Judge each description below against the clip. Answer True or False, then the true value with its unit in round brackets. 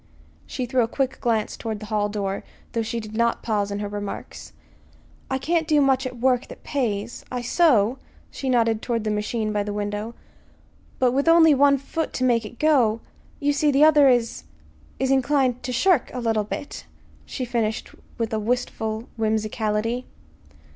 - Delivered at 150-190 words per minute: True (175 wpm)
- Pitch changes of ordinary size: True (3.7 semitones)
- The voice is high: True (235 Hz)